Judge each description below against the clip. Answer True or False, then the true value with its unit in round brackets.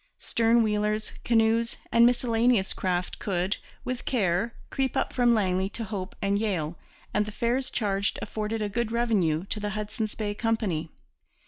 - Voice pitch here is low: False (215 Hz)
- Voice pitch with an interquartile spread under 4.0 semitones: True (2.9 semitones)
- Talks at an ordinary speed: True (155 wpm)